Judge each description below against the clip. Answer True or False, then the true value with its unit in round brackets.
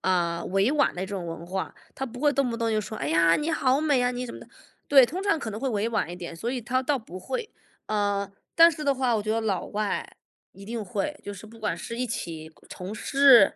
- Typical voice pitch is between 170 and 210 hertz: False (225 Hz)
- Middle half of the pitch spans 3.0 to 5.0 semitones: False (5.5 semitones)